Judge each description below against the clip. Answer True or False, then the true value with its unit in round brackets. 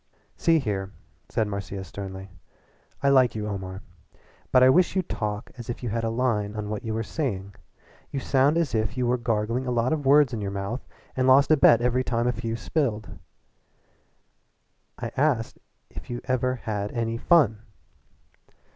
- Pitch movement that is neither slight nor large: True (3.7 semitones)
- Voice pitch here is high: False (115 Hz)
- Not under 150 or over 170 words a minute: False (185 wpm)